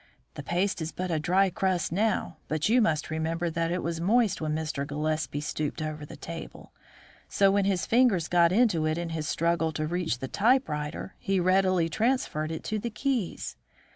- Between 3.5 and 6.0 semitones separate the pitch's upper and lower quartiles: Yes, average, 3.8 semitones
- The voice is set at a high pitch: No, medium, 170 Hz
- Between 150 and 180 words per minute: No, average, 195 wpm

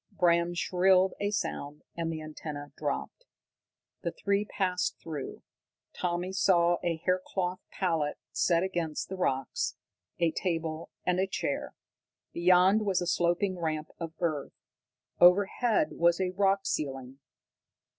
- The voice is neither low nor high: Yes, medium, 175 Hz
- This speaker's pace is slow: Yes, slow, 130 wpm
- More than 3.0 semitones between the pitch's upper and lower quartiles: No, average, 2.7 semitones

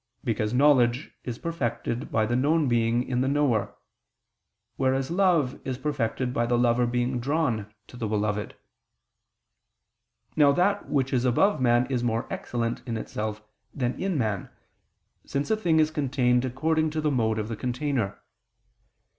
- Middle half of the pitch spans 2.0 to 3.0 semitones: No, average, 3.7 semitones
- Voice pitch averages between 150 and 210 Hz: No, low, 125 Hz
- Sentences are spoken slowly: No, average, 155 wpm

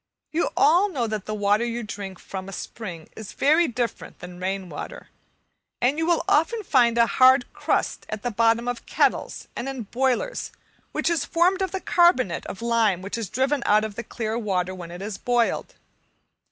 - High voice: Yes, high, 235 Hz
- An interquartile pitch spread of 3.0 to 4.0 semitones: No, average, 5.2 semitones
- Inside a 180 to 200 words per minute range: Yes, average, 195 wpm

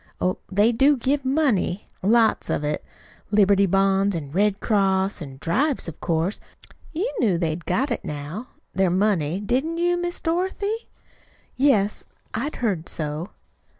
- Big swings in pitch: Yes, wide, 7.1 semitones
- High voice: Yes, high, 205 Hz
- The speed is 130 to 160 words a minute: Yes, average, 150 wpm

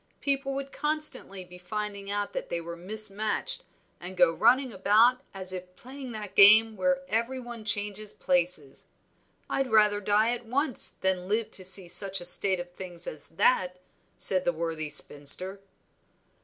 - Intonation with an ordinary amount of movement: Yes, average, 3.7 semitones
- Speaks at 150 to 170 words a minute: Yes, average, 160 wpm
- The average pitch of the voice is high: Yes, high, 200 Hz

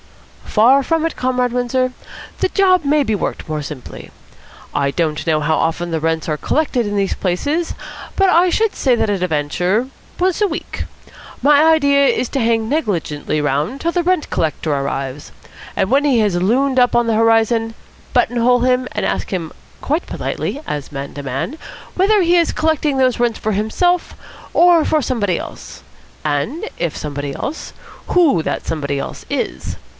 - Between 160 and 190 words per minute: Yes, average, 175 wpm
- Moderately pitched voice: No, high, 235 Hz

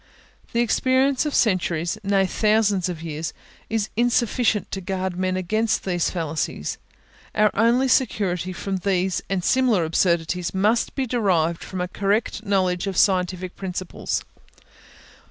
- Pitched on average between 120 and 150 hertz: No, high, 190 Hz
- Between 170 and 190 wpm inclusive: No, slow, 135 wpm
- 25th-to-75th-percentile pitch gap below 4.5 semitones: Yes, average, 3.6 semitones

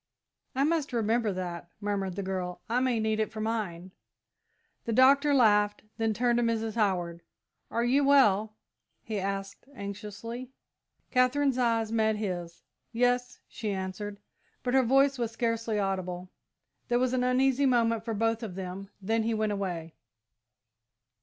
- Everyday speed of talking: Yes, average, 150 wpm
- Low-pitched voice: No, high, 220 Hz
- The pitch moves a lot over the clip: No, average, 3.8 semitones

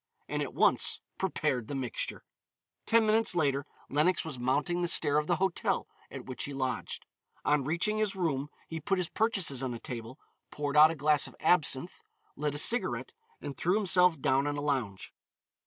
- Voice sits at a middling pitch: Yes, medium, 150 Hz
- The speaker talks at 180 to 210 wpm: Yes, average, 185 wpm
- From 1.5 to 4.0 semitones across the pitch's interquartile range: No, average, 4.7 semitones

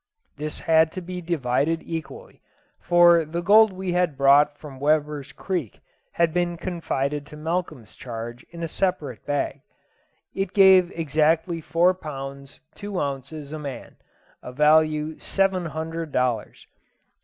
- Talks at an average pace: No, slow, 130 wpm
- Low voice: No, medium, 160 Hz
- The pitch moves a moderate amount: Yes, average, 3.5 semitones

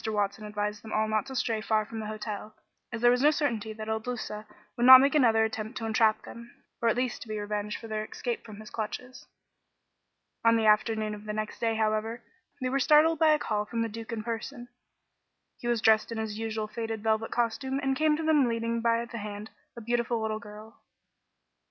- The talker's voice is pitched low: No, high, 225 Hz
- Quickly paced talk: Yes, fast, 220 wpm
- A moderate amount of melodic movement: No, narrow, 1.9 semitones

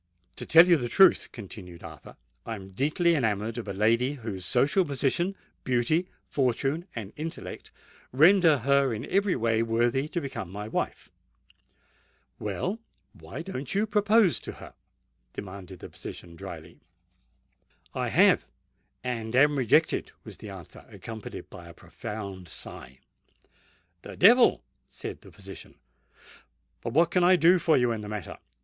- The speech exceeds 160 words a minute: No, average, 140 wpm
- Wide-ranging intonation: Yes, wide, 7.7 semitones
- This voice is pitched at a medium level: No, low, 125 Hz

